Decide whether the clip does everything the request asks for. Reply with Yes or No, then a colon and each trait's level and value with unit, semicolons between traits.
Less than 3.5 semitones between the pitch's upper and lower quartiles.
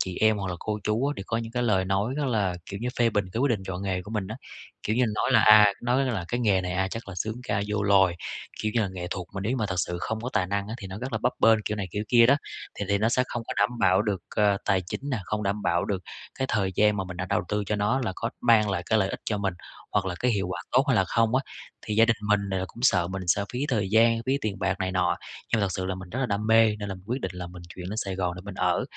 Yes: average, 3.1 semitones